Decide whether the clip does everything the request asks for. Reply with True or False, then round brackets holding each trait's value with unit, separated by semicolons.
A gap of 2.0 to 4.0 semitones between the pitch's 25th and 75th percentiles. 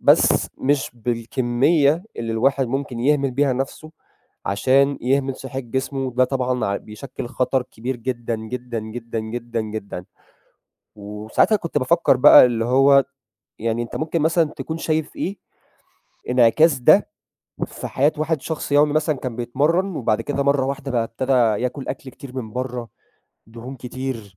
True (3.0 semitones)